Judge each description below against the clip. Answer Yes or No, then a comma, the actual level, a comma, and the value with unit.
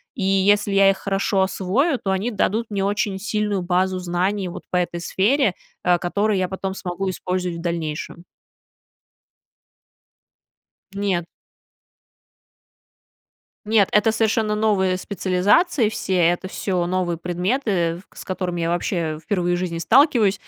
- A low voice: No, high, 190 Hz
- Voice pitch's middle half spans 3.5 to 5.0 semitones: No, average, 2.7 semitones